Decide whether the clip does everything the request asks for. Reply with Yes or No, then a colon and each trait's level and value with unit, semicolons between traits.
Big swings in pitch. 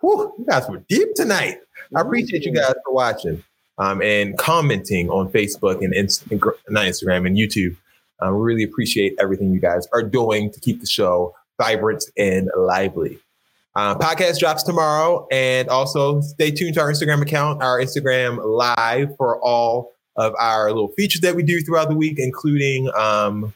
Yes: wide, 6.9 semitones